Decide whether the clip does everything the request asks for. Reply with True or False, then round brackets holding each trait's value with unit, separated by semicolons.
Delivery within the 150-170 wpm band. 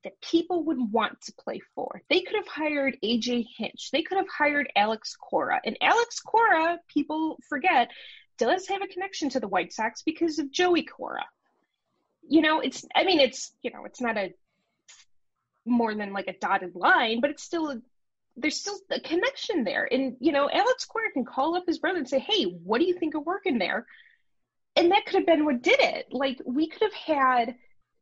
False (200 wpm)